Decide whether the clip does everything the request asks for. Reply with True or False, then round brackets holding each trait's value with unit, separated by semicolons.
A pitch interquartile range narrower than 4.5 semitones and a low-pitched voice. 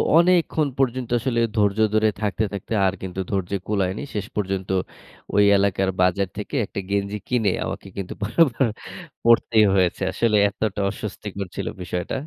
True (2.7 semitones; 105 Hz)